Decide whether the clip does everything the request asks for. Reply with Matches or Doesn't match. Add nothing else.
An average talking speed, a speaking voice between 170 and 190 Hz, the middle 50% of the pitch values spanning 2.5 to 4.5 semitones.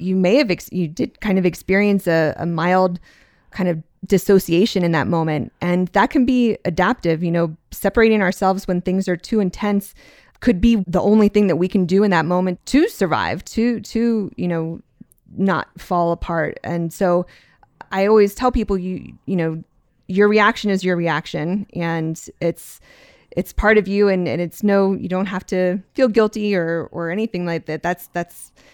Matches